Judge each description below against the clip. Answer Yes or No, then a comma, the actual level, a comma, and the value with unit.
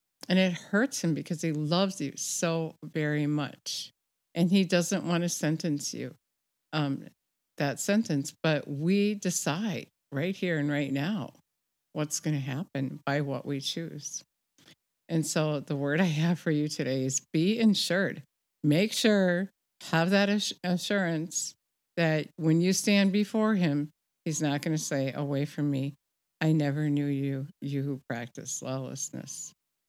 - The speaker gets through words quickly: No, average, 155 wpm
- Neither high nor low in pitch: Yes, medium, 155 Hz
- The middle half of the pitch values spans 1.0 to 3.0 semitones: No, average, 3.8 semitones